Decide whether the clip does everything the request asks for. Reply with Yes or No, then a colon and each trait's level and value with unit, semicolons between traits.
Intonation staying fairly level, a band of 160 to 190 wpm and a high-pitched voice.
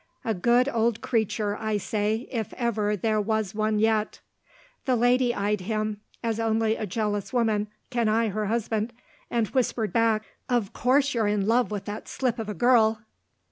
Yes: narrow, 2.0 semitones; average, 175 wpm; high, 220 Hz